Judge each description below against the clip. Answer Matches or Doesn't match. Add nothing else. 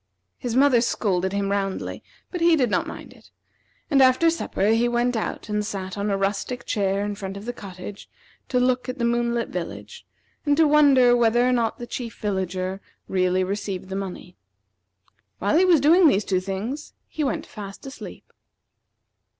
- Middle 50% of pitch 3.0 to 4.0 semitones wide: Doesn't match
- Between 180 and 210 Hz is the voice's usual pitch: Doesn't match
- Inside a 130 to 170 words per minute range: Doesn't match